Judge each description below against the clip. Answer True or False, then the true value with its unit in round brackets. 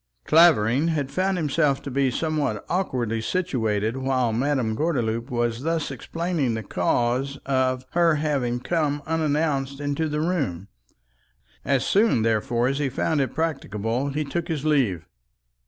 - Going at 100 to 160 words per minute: True (140 wpm)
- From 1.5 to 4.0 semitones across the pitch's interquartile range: False (4.6 semitones)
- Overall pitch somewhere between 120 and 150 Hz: True (140 Hz)